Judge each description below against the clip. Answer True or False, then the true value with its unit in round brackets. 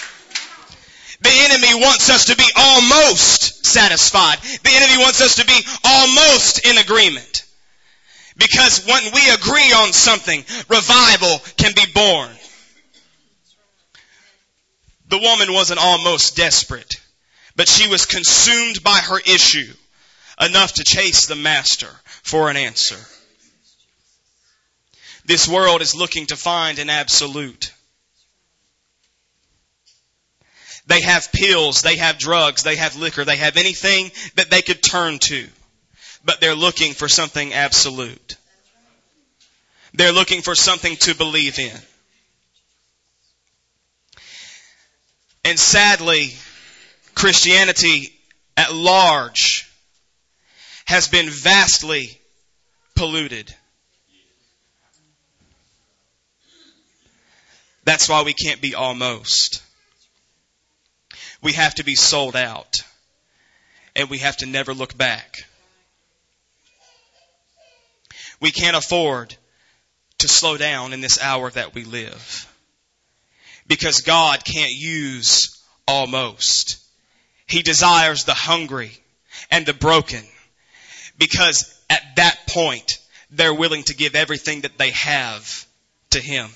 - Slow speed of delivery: True (105 wpm)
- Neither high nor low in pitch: True (155 Hz)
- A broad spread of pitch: True (5.7 semitones)